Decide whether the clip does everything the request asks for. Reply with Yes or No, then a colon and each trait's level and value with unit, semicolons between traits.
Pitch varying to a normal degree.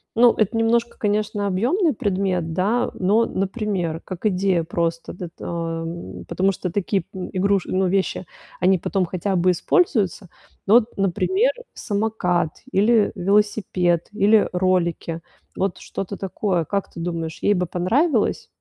Yes: average, 3.0 semitones